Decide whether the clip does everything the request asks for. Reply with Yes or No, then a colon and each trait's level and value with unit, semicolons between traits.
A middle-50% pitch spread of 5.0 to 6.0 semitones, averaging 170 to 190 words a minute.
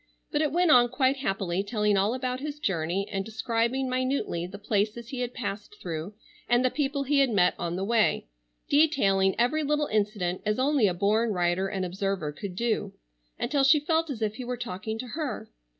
No: average, 5.3 semitones; average, 200 wpm